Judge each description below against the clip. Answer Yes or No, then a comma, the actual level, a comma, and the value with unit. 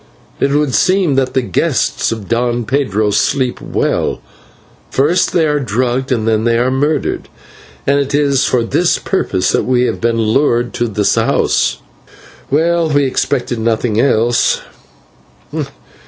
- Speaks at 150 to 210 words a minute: No, average, 140 wpm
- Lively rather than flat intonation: No, average, 3.6 semitones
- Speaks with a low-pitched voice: Yes, low, 125 Hz